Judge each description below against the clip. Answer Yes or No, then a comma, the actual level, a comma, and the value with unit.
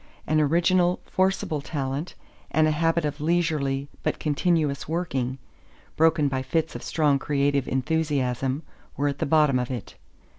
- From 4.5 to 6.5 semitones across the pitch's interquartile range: No, average, 2.9 semitones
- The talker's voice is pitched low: No, medium, 150 Hz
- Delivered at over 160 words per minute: No, average, 145 wpm